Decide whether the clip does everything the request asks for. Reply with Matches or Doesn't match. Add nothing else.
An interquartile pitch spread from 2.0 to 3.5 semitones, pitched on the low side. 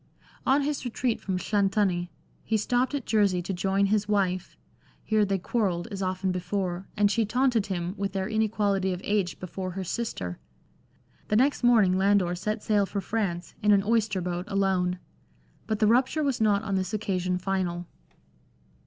Doesn't match